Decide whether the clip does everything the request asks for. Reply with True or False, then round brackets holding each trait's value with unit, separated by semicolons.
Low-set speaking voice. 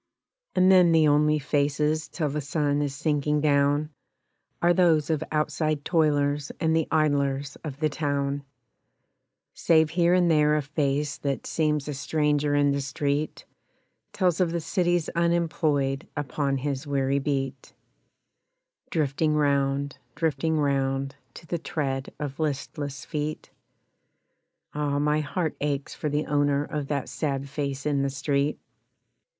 False (145 Hz)